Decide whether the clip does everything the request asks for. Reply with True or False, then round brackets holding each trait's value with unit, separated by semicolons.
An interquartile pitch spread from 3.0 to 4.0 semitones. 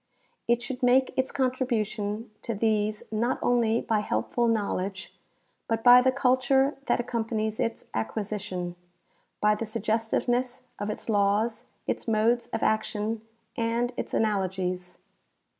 False (2.5 semitones)